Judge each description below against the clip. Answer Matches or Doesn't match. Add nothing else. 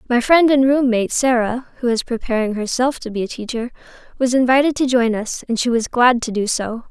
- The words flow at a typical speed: Doesn't match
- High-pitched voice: Matches